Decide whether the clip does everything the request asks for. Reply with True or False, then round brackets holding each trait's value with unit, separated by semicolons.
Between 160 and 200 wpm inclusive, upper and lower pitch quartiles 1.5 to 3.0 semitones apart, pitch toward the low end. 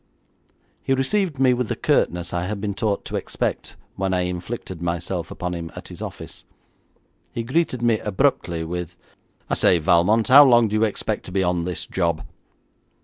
False (180 wpm; 5.2 semitones; 95 Hz)